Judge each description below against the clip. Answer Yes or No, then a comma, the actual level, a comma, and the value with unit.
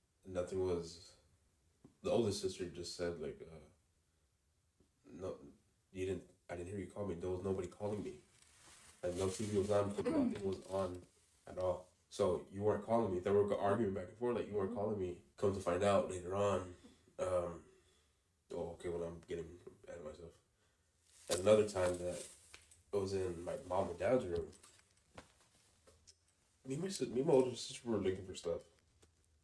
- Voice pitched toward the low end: Yes, very low, 90 Hz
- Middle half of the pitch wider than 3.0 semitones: No, narrow, 2.6 semitones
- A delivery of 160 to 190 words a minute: Yes, average, 175 wpm